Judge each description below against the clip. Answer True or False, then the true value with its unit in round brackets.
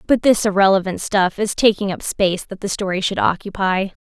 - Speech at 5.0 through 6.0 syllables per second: True (5.5 syllables/s)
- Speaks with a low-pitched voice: False (195 Hz)